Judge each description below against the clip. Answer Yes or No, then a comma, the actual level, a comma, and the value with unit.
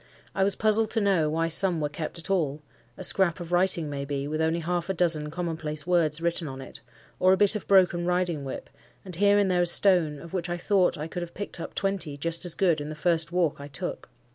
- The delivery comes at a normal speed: No, fast, 245 wpm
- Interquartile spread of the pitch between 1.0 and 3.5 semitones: Yes, average, 3.1 semitones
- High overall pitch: No, medium, 170 Hz